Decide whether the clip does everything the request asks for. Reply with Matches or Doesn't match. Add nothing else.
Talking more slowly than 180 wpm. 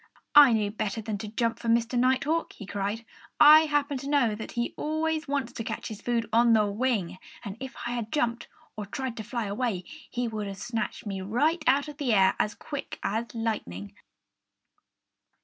Doesn't match